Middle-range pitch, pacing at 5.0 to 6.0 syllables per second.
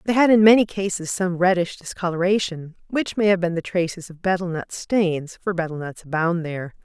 Yes: medium, 180 Hz; 5.4 syllables/s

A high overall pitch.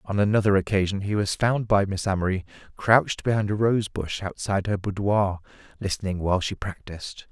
No: low, 100 Hz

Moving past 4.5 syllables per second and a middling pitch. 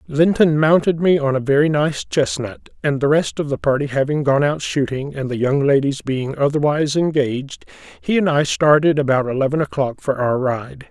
Yes: 5.2 syllables/s; medium, 145 Hz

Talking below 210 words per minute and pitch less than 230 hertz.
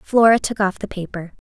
Yes: average, 200 wpm; high, 205 Hz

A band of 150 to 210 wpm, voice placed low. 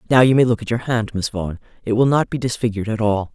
No: fast, 285 wpm; low, 115 Hz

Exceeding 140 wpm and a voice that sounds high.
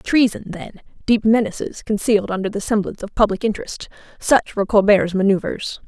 No: slow, 135 wpm; high, 210 Hz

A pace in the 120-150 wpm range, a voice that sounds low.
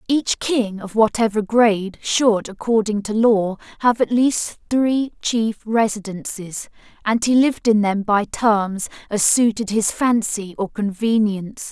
No: average, 145 wpm; high, 215 Hz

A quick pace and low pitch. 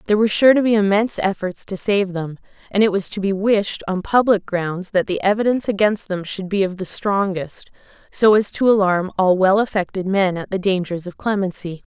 No: fast, 210 wpm; high, 195 Hz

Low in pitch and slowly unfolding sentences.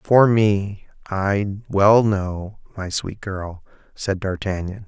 Yes: low, 100 Hz; slow, 125 wpm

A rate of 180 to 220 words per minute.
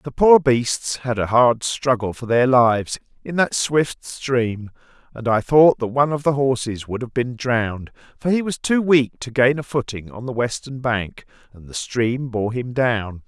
Yes: fast, 205 wpm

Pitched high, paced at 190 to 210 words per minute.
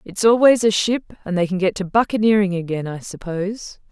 Yes: high, 195 Hz; average, 200 wpm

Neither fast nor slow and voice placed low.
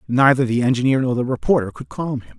No: fast, 225 wpm; low, 125 Hz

